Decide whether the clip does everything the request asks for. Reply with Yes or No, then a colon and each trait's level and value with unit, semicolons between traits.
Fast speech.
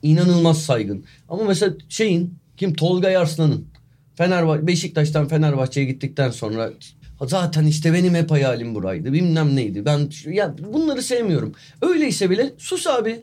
No: average, 130 wpm